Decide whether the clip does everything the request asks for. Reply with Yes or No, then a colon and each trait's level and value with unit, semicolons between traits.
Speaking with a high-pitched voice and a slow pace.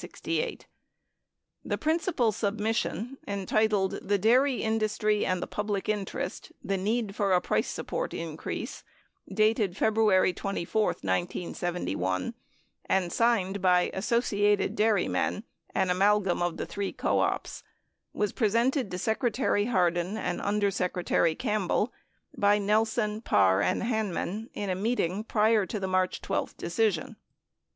Yes: high, 205 Hz; slow, 130 wpm